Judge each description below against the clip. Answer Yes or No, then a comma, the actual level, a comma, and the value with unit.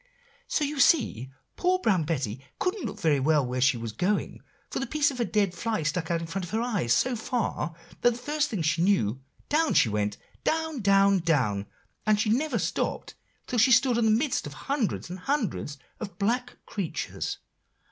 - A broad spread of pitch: Yes, wide, 8.6 semitones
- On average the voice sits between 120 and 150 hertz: No, high, 205 Hz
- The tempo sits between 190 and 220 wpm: Yes, average, 200 wpm